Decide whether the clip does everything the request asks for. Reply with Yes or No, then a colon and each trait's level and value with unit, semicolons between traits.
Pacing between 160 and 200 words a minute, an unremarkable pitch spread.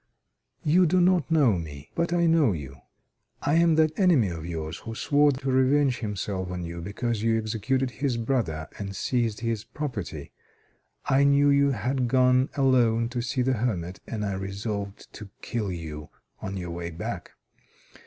No: average, 170 wpm; wide, 6.1 semitones